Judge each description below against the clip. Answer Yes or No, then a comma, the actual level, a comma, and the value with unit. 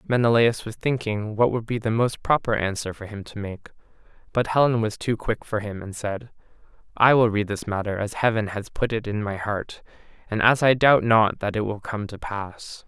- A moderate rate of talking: No, fast, 220 wpm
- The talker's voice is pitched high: No, low, 110 Hz